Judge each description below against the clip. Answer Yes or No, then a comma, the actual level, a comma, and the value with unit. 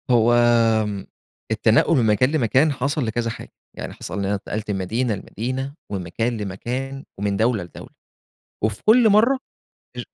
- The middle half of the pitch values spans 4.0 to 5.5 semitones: Yes, average, 4.6 semitones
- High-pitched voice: No, low, 115 Hz